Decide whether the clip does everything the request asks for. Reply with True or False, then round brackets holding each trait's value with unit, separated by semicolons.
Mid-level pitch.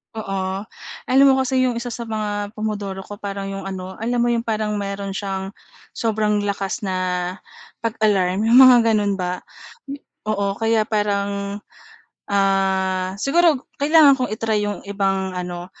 False (205 Hz)